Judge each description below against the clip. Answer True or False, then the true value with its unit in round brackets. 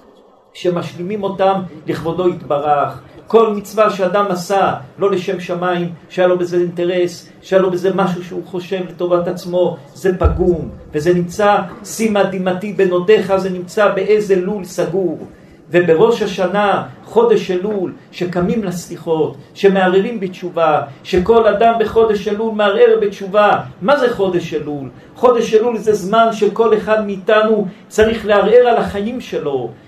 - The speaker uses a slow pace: False (130 wpm)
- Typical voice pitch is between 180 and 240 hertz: True (190 Hz)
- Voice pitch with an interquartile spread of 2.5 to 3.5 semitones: True (3.2 semitones)